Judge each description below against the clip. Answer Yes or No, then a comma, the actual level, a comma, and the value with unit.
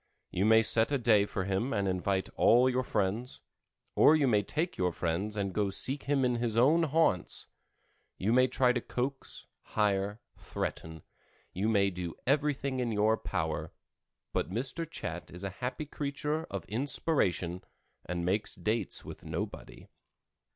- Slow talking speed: No, average, 160 wpm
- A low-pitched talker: Yes, low, 110 Hz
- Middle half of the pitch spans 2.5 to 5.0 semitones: No, wide, 5.5 semitones